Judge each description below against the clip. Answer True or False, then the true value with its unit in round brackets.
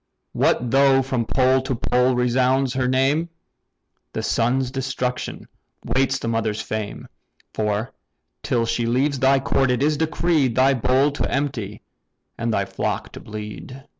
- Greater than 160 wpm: False (145 wpm)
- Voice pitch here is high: False (130 Hz)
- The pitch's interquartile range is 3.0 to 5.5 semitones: False (2.5 semitones)